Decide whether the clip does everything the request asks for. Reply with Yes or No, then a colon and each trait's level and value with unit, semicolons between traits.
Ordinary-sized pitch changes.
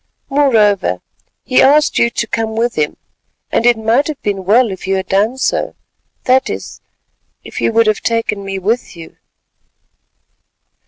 Yes: average, 4.0 semitones